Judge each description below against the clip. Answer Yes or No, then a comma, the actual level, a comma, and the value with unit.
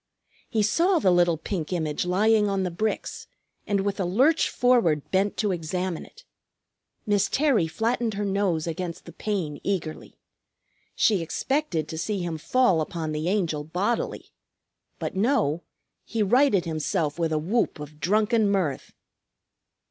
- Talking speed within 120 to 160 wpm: Yes, average, 150 wpm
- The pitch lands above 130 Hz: Yes, high, 190 Hz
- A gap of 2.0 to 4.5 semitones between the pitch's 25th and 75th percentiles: No, average, 4.9 semitones